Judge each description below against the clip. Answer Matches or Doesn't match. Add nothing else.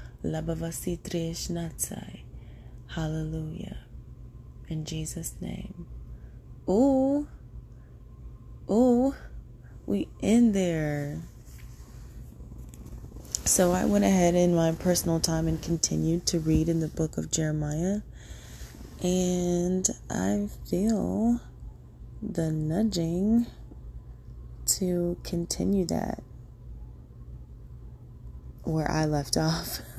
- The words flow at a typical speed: Doesn't match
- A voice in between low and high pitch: Matches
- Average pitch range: Matches